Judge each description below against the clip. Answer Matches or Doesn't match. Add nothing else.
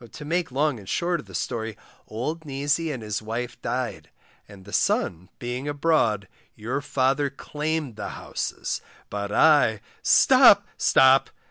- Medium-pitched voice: Doesn't match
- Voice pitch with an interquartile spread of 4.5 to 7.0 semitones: Matches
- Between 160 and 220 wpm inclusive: Doesn't match